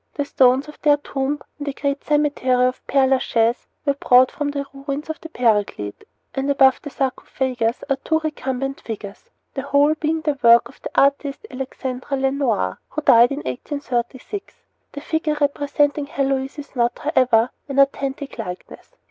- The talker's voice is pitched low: No, very high, 275 Hz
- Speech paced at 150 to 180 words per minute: Yes, average, 165 wpm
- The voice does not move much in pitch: Yes, narrow, 2.3 semitones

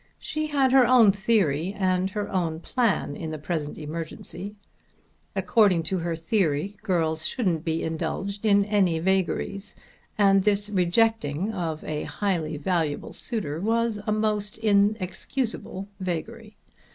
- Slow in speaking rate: Yes, slow, 130 wpm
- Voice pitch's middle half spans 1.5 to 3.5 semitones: No, average, 4.4 semitones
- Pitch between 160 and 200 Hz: Yes, high, 190 Hz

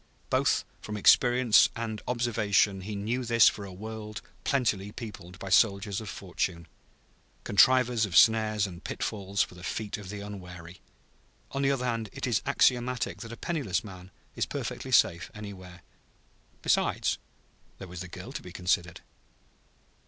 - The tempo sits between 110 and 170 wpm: Yes, average, 150 wpm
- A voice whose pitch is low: Yes, low, 105 Hz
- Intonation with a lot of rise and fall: No, average, 3.8 semitones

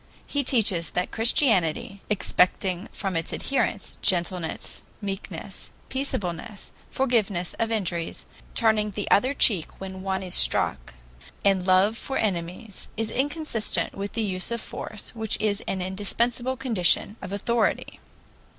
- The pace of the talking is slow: Yes, slow, 130 wpm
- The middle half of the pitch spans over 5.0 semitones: No, average, 3.6 semitones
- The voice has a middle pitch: No, high, 205 Hz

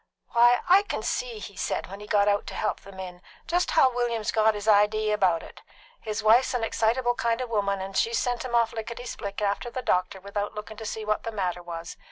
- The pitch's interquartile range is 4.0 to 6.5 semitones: No, average, 3.0 semitones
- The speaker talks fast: Yes, fast, 240 wpm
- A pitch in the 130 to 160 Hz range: No, high, 215 Hz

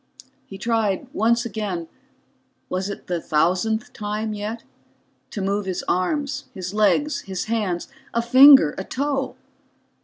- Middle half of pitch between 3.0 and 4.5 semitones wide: Yes, average, 3.7 semitones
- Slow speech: Yes, slow, 130 wpm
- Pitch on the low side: No, high, 210 Hz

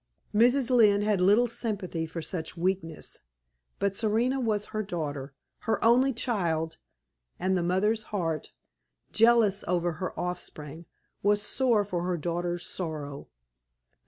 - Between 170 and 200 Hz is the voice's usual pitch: Yes, high, 190 Hz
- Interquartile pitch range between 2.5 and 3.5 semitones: No, average, 4.4 semitones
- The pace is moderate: No, slow, 130 wpm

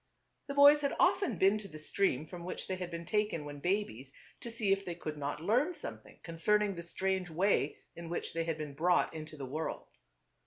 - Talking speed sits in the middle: No, fast, 210 wpm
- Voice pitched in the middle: Yes, medium, 175 Hz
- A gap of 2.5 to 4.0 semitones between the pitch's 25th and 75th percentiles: No, average, 4.8 semitones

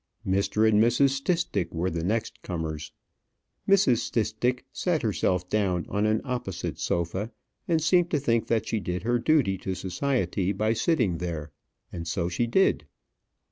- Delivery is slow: No, average, 155 wpm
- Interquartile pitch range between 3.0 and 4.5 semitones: No, wide, 5.6 semitones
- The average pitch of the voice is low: Yes, low, 110 Hz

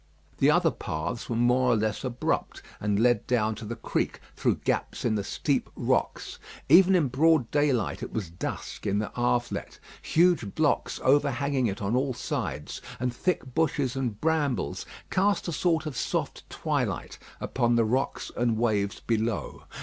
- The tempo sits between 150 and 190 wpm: Yes, average, 165 wpm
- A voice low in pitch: Yes, low, 125 Hz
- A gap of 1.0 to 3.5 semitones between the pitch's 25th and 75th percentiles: No, average, 4.6 semitones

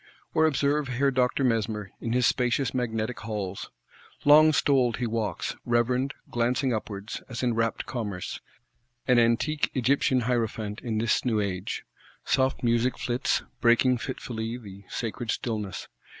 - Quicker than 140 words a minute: No, slow, 135 wpm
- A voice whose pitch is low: Yes, low, 120 Hz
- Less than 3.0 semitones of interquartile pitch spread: Yes, narrow, 2.5 semitones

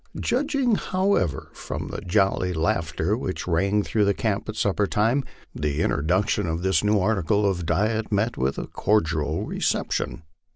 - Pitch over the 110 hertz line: No, low, 100 Hz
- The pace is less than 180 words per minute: Yes, average, 150 wpm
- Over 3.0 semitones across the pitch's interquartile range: Yes, average, 4.5 semitones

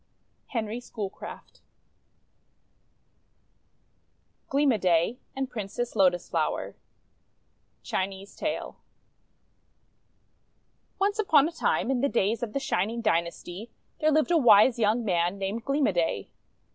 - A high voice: Yes, high, 225 Hz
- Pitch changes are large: Yes, wide, 5.7 semitones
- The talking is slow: Yes, slow, 115 wpm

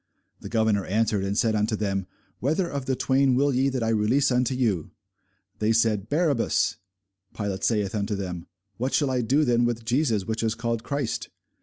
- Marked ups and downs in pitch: No, average, 3.8 semitones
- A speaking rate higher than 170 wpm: Yes, average, 185 wpm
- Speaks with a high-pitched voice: No, low, 115 Hz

